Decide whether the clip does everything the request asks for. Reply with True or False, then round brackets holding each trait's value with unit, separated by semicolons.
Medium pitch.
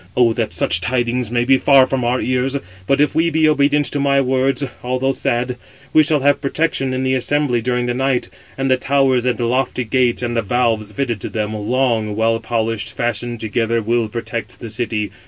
False (125 Hz)